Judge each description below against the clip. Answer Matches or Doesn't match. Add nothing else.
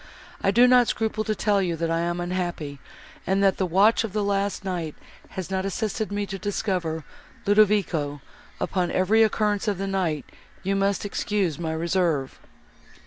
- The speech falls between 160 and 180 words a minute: Matches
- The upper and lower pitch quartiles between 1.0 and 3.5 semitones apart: Matches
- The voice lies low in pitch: Doesn't match